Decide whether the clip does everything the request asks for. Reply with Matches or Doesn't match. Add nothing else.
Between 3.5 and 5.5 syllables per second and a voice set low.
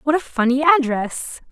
Doesn't match